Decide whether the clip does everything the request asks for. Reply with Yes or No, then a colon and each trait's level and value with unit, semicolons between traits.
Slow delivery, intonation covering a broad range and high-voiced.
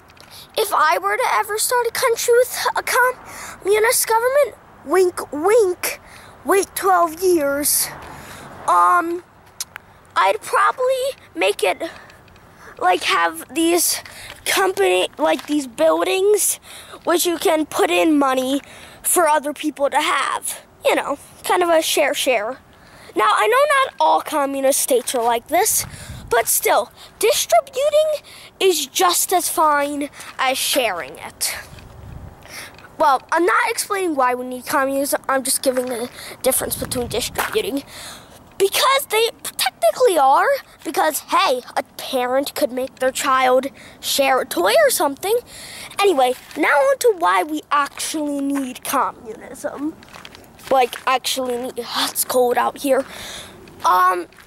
Yes: slow, 125 wpm; wide, 6.1 semitones; very high, 300 Hz